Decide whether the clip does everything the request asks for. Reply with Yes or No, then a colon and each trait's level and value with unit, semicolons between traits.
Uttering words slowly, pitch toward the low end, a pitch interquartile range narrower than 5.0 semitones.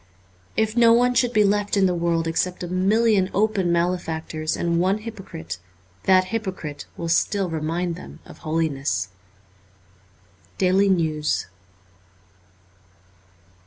No: slow, 125 wpm; medium, 180 Hz; average, 4.0 semitones